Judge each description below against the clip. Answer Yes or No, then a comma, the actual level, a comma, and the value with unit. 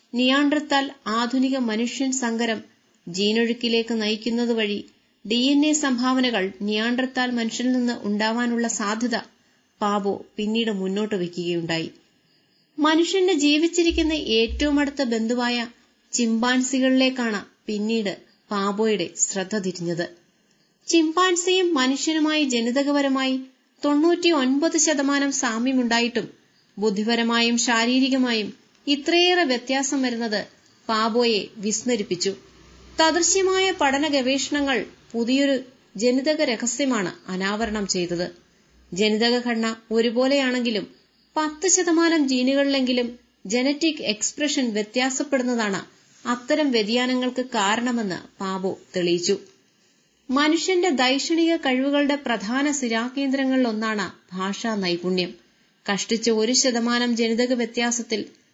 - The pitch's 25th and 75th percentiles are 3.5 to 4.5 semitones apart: Yes, average, 4.2 semitones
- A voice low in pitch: No, high, 240 Hz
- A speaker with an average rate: Yes, average, 80 wpm